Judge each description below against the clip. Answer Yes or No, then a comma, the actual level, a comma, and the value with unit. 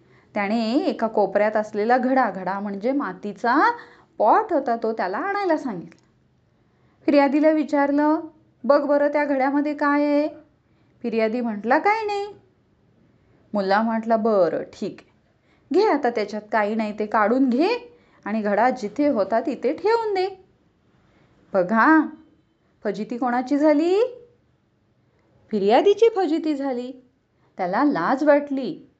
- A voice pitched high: Yes, very high, 275 Hz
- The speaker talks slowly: Yes, slow, 115 wpm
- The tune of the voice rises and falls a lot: Yes, wide, 5.7 semitones